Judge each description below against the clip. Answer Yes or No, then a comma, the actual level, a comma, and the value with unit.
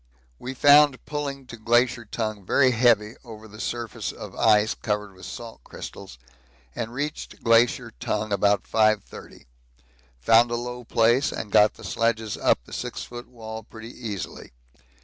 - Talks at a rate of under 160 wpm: Yes, average, 150 wpm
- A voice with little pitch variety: Yes, narrow, 2.3 semitones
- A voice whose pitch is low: Yes, low, 115 Hz